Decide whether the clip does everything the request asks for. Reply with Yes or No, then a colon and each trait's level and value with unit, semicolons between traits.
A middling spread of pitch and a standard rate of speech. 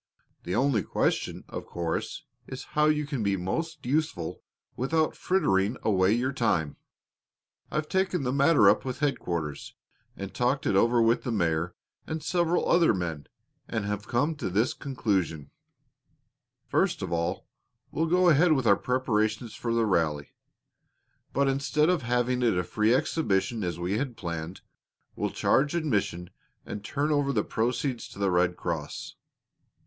No: wide, 7.3 semitones; average, 155 wpm